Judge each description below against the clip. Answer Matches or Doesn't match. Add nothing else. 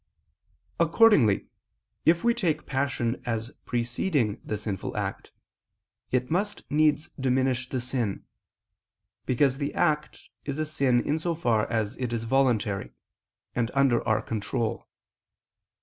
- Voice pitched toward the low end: Matches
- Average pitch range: Matches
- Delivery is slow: Matches